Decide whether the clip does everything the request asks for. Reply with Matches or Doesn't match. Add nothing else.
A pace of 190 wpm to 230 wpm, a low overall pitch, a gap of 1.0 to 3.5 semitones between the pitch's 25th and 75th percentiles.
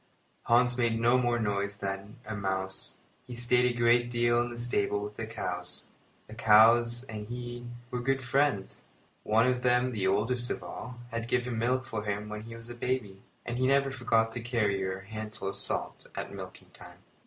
Matches